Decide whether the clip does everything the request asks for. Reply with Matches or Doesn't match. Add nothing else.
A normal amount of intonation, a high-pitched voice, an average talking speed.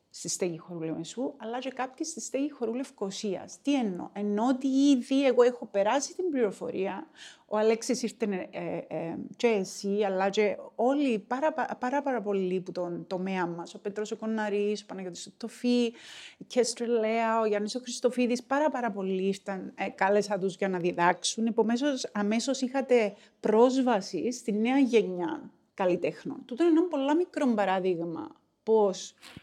Matches